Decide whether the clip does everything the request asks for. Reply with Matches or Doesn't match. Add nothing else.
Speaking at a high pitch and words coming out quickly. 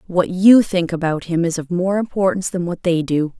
Doesn't match